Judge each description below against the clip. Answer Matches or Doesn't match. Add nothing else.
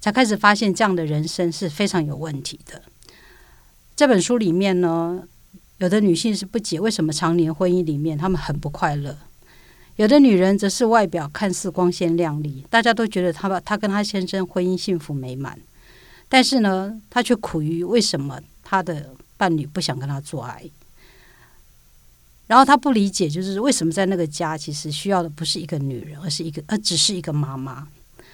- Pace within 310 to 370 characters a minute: Doesn't match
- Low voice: Doesn't match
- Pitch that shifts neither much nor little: Matches